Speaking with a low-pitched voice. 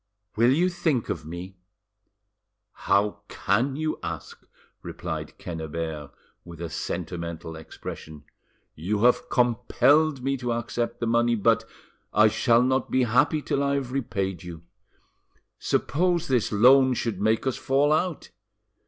Yes: low, 120 Hz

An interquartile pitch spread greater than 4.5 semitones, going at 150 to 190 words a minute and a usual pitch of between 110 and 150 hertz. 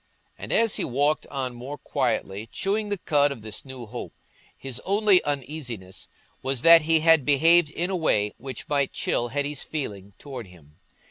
Yes: average, 5.0 semitones; average, 175 wpm; medium, 140 Hz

